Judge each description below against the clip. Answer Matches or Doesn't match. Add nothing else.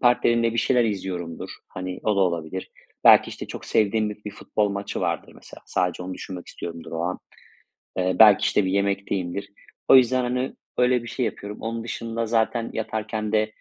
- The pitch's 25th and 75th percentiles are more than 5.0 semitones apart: Doesn't match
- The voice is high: Doesn't match